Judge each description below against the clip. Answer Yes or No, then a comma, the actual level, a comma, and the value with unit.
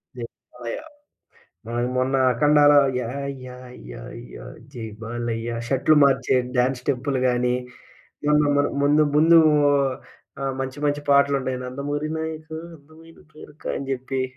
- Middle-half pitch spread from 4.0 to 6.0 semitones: No, average, 2.9 semitones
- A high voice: No, low, 135 Hz